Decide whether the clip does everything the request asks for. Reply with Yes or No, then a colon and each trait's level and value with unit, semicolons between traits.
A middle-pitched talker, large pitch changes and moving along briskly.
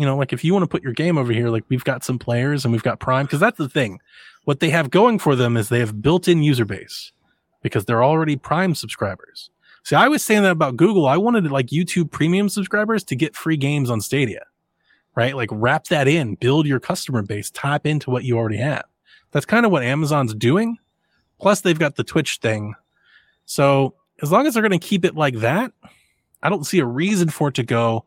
Yes: medium, 145 Hz; wide, 6.2 semitones; fast, 230 wpm